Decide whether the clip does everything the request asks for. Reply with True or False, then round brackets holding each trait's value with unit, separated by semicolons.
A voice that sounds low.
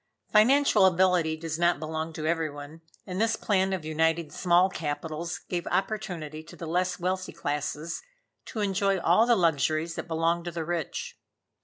False (170 Hz)